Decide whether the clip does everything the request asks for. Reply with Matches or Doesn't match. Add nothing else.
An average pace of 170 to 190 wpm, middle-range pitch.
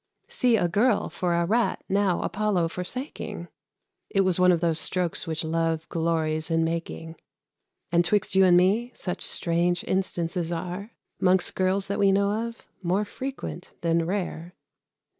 Doesn't match